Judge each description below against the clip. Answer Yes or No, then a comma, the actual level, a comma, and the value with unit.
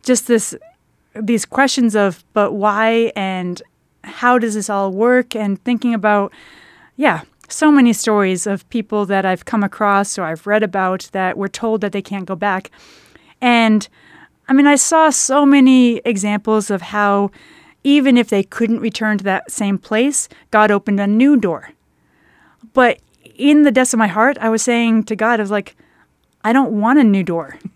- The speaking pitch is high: Yes, high, 220 Hz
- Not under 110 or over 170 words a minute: No, average, 180 wpm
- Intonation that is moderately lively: Yes, average, 3.4 semitones